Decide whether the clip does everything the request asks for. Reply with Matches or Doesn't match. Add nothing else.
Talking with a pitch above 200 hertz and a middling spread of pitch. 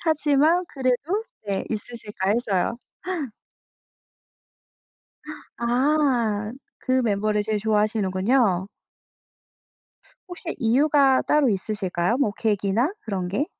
Matches